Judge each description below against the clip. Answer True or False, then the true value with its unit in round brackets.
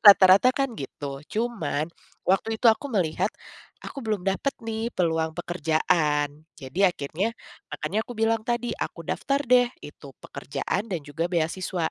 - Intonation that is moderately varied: False (6.2 semitones)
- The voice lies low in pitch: False (185 Hz)